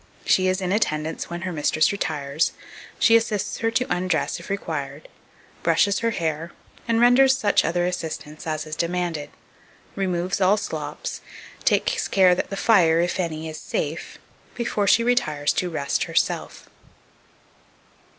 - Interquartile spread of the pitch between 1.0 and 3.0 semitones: No, average, 4.6 semitones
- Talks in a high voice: No, medium, 180 Hz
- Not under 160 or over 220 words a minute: No, average, 145 wpm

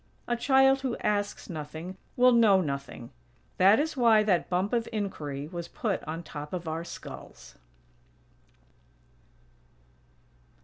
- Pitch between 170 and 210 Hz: Yes, high, 190 Hz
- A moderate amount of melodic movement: No, wide, 6.5 semitones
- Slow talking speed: Yes, slow, 125 wpm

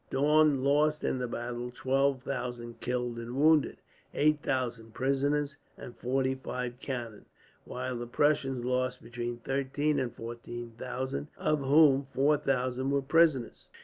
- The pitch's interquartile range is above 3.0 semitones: No, narrow, 2.5 semitones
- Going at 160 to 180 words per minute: No, average, 140 wpm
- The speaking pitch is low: Yes, low, 130 Hz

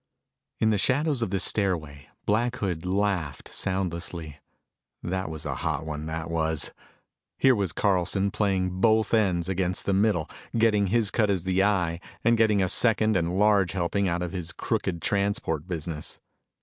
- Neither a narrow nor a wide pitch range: Yes, average, 3.4 semitones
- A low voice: Yes, very low, 95 Hz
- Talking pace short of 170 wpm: Yes, average, 160 wpm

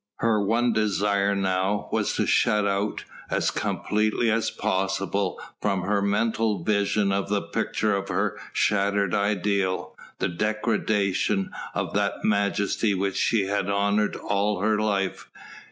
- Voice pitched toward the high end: No, low, 100 Hz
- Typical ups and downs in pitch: No, narrow, 1.4 semitones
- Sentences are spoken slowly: Yes, slow, 130 wpm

